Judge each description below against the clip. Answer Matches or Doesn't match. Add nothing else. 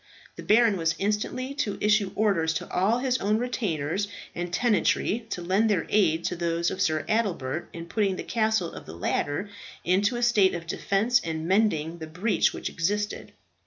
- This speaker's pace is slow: Doesn't match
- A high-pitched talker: Matches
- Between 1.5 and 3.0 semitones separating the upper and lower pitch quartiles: Doesn't match